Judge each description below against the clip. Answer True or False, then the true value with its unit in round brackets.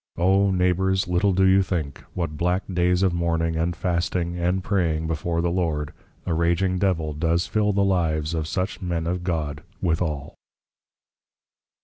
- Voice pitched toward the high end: False (85 Hz)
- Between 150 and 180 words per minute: True (155 wpm)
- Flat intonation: True (2.2 semitones)